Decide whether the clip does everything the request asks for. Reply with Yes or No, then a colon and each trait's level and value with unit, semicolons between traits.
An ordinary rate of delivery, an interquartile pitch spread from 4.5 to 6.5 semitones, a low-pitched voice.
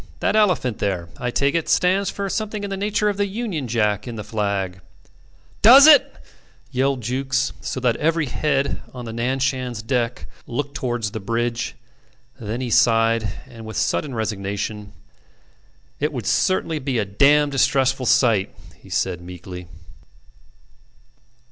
Yes: average, 155 wpm; average, 5.1 semitones; low, 125 Hz